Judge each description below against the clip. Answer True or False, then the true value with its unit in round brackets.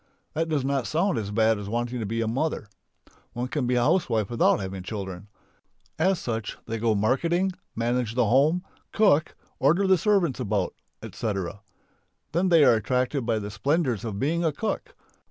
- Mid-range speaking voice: False (125 Hz)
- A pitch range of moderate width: False (6.6 semitones)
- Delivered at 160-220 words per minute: True (175 wpm)